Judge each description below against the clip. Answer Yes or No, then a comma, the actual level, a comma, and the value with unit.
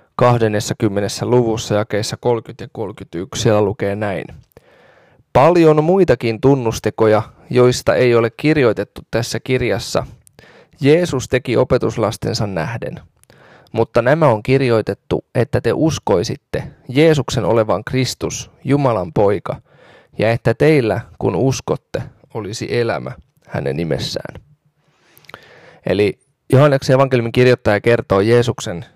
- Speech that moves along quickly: No, average, 100 wpm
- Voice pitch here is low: Yes, low, 120 Hz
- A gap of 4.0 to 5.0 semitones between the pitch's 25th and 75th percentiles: No, average, 3.6 semitones